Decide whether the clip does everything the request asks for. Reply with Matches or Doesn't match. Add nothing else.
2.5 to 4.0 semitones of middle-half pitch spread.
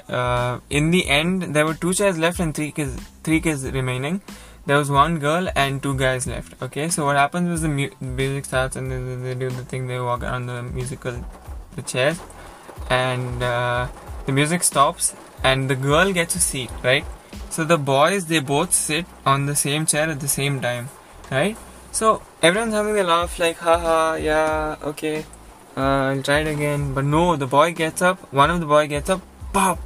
Matches